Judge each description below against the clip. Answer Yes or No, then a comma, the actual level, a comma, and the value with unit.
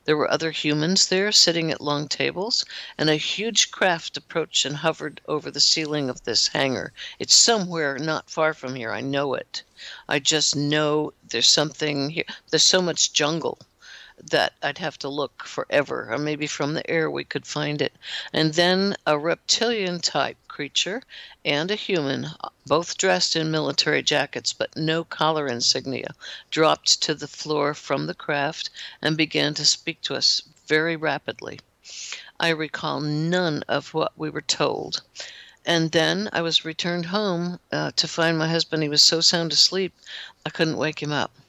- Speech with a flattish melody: Yes, narrow, 2.2 semitones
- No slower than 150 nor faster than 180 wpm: Yes, average, 170 wpm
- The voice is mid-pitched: Yes, medium, 155 Hz